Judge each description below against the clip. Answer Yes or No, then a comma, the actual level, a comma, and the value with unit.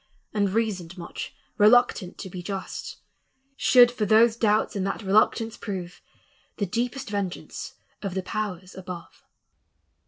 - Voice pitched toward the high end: Yes, high, 205 Hz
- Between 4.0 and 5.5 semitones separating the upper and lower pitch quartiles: No, average, 3.2 semitones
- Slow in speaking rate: Yes, slow, 130 wpm